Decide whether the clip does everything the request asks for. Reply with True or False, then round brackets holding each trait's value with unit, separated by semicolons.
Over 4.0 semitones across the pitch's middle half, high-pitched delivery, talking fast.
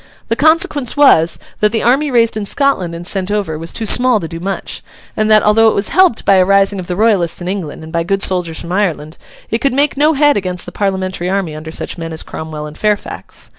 True (5.0 semitones; 195 Hz; 240 wpm)